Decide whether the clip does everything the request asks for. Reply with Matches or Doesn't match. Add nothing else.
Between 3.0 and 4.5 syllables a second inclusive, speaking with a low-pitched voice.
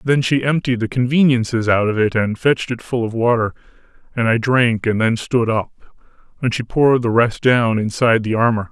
Doesn't match